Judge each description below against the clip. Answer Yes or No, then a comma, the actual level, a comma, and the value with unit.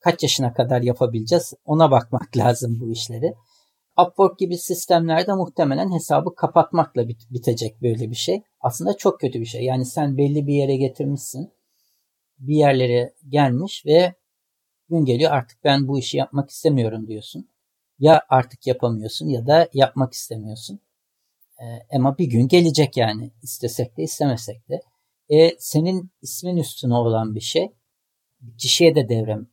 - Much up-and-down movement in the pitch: No, average, 5.0 semitones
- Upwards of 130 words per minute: Yes, fast, 140 wpm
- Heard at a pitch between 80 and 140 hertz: Yes, low, 135 Hz